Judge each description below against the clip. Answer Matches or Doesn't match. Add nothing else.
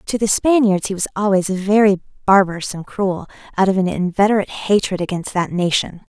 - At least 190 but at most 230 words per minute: Doesn't match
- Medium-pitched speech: Doesn't match